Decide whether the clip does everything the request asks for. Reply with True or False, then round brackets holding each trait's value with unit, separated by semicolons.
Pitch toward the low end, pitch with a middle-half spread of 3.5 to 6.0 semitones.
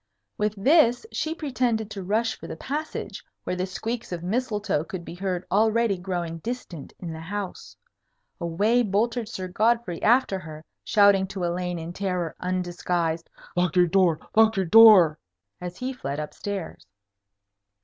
False (190 Hz; 4.2 semitones)